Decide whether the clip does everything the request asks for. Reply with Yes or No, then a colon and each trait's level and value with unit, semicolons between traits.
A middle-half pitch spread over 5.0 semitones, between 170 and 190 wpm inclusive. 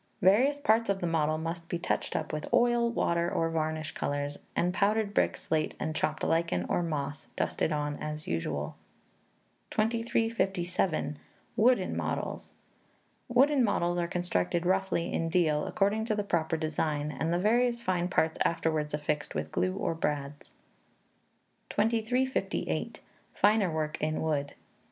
No: wide, 5.5 semitones; average, 140 wpm